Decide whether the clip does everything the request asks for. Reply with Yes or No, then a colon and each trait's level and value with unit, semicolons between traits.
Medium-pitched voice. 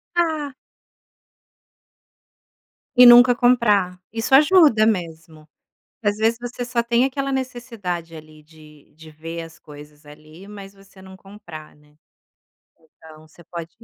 No: high, 195 Hz